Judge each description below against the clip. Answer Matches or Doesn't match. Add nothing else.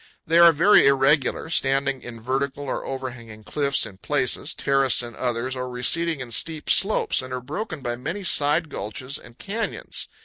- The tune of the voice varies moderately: Matches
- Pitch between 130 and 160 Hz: Matches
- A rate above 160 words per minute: Matches